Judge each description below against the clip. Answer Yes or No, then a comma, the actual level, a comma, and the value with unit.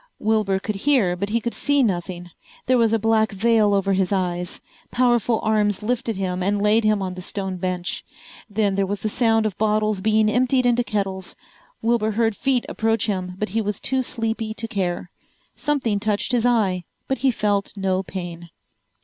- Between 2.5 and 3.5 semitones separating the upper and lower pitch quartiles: Yes, average, 2.9 semitones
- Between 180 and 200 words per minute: Yes, average, 185 wpm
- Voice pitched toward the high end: Yes, high, 210 Hz